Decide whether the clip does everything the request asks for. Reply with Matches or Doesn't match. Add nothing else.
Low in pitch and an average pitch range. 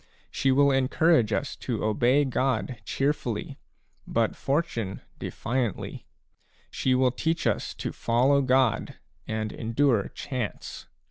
Matches